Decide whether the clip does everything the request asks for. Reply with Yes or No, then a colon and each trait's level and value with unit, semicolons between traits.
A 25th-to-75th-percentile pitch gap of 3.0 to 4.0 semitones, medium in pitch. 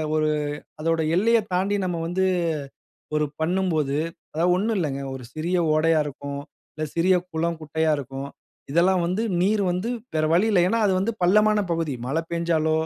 Yes: average, 3.3 semitones; medium, 170 Hz